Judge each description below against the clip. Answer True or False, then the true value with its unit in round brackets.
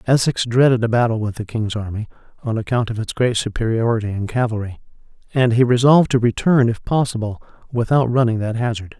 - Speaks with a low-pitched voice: True (115 Hz)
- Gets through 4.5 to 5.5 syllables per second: False (6.0 syllables/s)